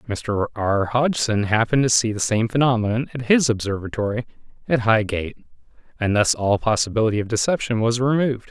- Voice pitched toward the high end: No, low, 115 Hz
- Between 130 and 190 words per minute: Yes, average, 155 wpm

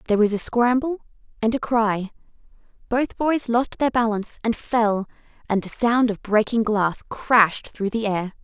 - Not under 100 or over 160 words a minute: No, average, 170 wpm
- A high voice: Yes, high, 225 Hz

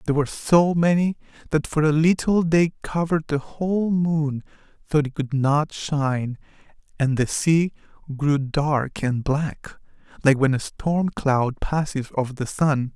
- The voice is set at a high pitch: No, medium, 150 Hz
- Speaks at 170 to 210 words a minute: No, average, 155 wpm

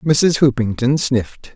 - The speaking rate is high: No, slow, 115 wpm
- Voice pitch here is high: No, low, 130 Hz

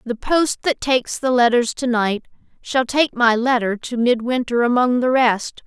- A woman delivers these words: Yes, female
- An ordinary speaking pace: Yes, average, 180 wpm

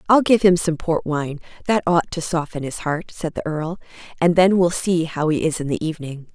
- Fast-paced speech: Yes, fast, 235 wpm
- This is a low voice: No, medium, 165 Hz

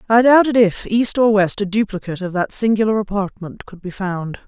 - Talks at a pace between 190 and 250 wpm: Yes, average, 200 wpm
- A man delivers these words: No, female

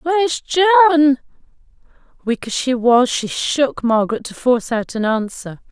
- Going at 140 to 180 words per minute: Yes, average, 145 wpm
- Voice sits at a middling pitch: No, very high, 255 Hz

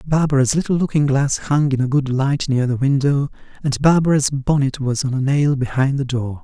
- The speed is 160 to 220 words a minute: Yes, fast, 205 wpm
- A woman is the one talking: No, male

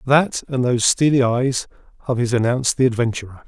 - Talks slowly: No, average, 175 wpm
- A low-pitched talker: Yes, low, 125 Hz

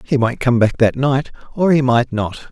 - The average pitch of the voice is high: No, low, 125 Hz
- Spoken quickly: Yes, fast, 240 wpm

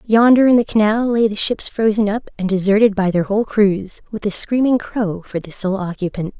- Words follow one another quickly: Yes, fast, 215 wpm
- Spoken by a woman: Yes, female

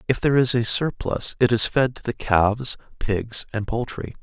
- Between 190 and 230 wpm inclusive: Yes, average, 200 wpm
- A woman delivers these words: No, male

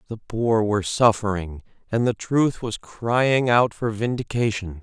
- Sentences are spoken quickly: No, average, 150 wpm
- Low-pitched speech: Yes, low, 110 Hz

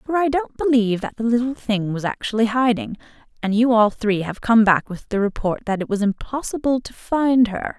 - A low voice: No, high, 230 Hz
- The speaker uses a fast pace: Yes, fast, 215 wpm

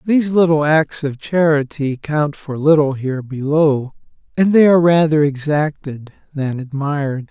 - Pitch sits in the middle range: Yes, medium, 150 Hz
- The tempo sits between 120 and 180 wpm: Yes, average, 140 wpm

